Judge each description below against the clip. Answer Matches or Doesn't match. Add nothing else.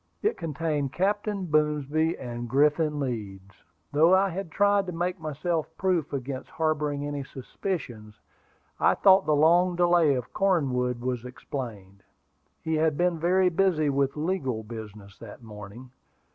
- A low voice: Doesn't match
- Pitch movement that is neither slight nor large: Doesn't match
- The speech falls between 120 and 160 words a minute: Matches